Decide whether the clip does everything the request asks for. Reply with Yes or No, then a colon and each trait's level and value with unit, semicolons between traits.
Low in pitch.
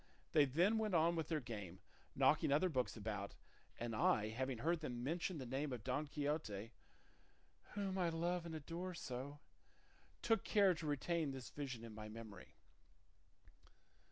No: medium, 145 Hz